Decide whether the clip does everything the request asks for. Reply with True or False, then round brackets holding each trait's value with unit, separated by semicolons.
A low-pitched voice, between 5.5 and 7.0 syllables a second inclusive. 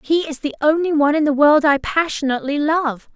False (295 Hz; 5.8 syllables/s)